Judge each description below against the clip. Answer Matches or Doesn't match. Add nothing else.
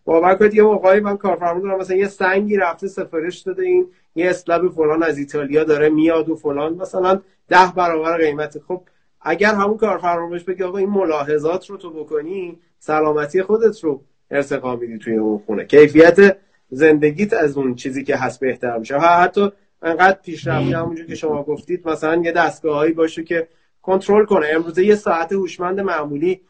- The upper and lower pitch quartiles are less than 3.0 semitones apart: Doesn't match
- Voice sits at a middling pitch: Matches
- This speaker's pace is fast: Matches